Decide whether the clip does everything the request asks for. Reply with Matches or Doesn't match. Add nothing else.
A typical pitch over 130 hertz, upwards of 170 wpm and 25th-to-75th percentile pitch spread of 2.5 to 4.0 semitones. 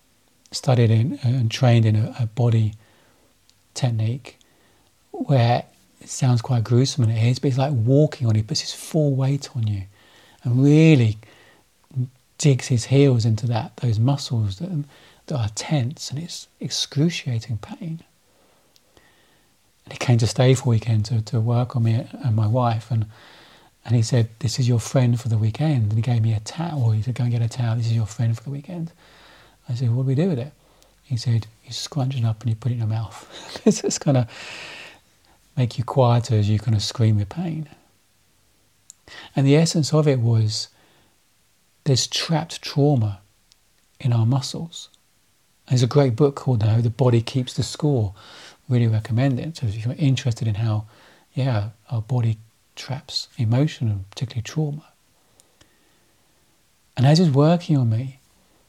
Doesn't match